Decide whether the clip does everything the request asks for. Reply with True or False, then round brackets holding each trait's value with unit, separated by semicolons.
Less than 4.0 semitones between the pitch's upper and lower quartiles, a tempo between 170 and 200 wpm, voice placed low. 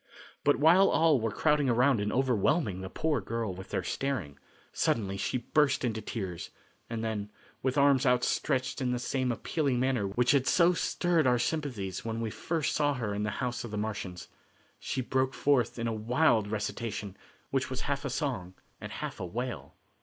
False (4.7 semitones; 185 wpm; 125 Hz)